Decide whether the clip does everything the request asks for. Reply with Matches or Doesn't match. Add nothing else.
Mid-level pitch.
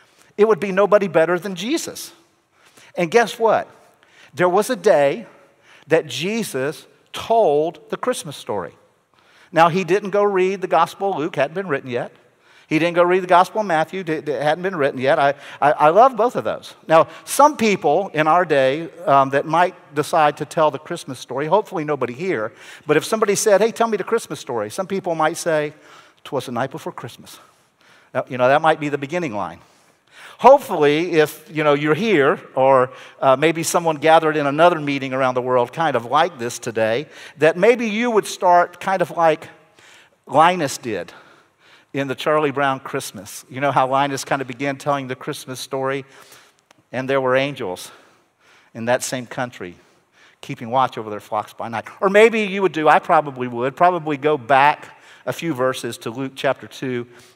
Matches